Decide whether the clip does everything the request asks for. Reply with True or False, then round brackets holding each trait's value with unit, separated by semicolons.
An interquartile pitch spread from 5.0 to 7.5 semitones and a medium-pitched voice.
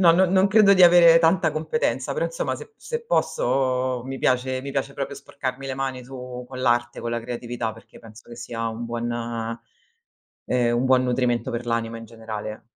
False (5.3 semitones; 130 Hz)